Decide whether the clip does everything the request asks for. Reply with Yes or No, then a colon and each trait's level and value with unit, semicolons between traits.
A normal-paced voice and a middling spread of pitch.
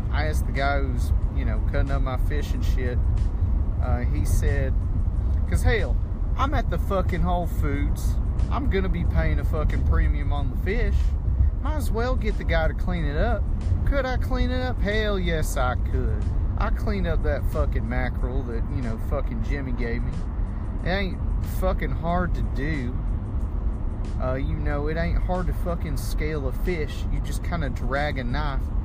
Yes: average, 190 wpm; average, 3.3 semitones